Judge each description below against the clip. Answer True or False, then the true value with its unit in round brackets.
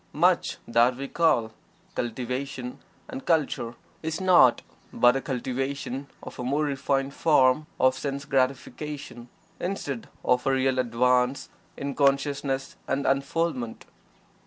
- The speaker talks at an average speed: False (120 wpm)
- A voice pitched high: False (135 Hz)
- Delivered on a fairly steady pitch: True (2.2 semitones)